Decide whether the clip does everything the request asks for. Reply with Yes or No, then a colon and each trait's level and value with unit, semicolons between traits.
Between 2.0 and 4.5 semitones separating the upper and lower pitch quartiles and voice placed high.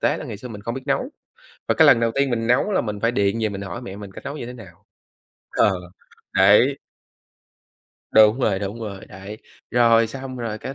No: average, 3.3 semitones; low, 115 Hz